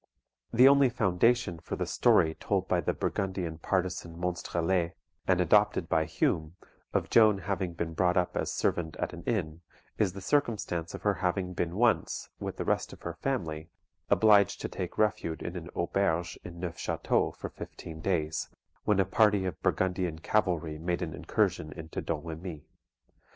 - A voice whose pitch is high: No, very low, 90 Hz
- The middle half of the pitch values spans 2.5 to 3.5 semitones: Yes, average, 3.2 semitones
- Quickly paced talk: No, average, 165 wpm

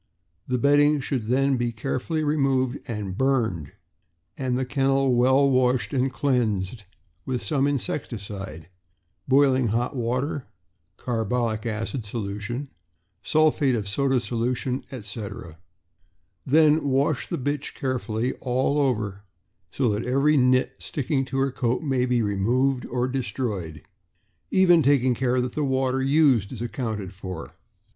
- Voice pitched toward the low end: Yes, low, 125 Hz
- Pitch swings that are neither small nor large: Yes, average, 3.3 semitones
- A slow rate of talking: Yes, slow, 130 wpm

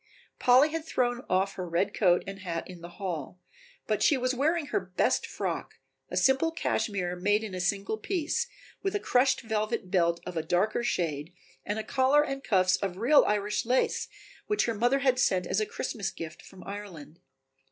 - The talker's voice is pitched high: Yes, high, 205 Hz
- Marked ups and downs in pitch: Yes, wide, 5.9 semitones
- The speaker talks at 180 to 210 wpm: Yes, average, 190 wpm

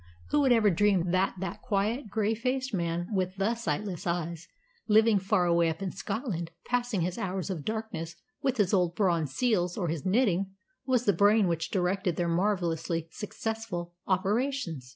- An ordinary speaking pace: Yes, average, 170 wpm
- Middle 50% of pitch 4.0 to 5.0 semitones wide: Yes, average, 4.3 semitones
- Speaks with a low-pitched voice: No, high, 190 Hz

